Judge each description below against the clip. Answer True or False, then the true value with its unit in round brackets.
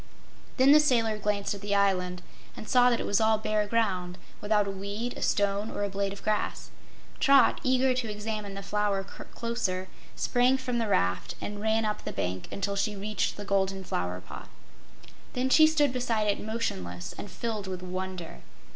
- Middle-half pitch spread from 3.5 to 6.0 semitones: False (2.9 semitones)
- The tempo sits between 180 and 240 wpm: True (185 wpm)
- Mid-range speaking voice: False (205 Hz)